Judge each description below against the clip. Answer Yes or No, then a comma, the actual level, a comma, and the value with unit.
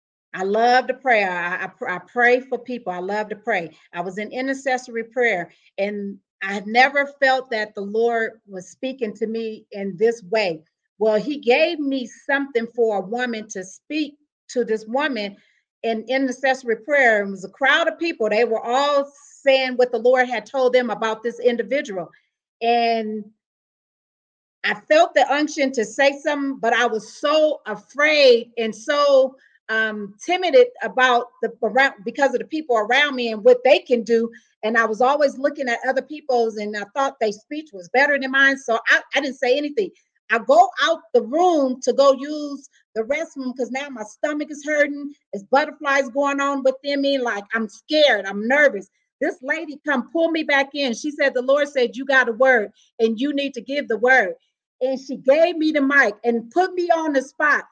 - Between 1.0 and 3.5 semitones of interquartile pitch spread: No, average, 4.0 semitones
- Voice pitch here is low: No, very high, 255 Hz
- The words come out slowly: No, average, 195 wpm